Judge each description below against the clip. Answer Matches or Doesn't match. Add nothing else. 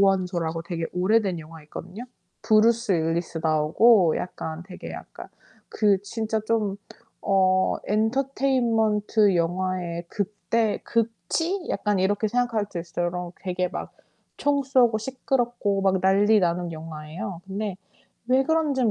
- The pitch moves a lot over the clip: Doesn't match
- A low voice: Doesn't match